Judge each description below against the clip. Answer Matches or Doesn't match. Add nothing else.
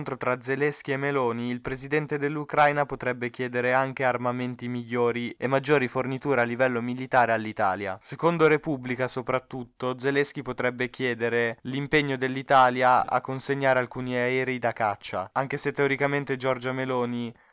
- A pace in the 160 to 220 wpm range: Doesn't match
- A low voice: Matches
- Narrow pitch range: Matches